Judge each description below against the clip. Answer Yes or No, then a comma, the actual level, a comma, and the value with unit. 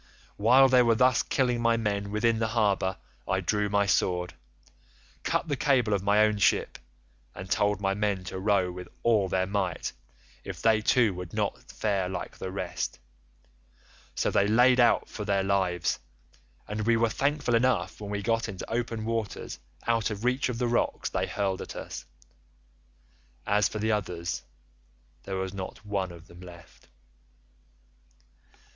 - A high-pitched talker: No, low, 105 Hz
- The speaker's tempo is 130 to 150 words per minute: No, average, 165 wpm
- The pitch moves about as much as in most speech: Yes, average, 3.4 semitones